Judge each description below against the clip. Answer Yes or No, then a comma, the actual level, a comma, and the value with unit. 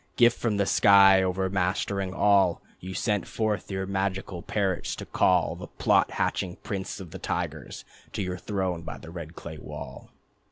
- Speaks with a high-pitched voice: No, very low, 95 Hz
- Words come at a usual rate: Yes, average, 165 wpm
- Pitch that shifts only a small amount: Yes, narrow, 1.7 semitones